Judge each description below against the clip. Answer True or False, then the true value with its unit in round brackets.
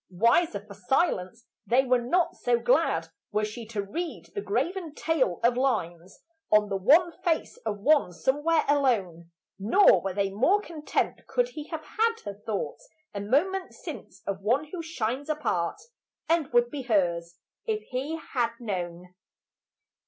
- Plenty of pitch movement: True (8.1 semitones)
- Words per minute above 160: False (155 wpm)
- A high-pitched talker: True (245 Hz)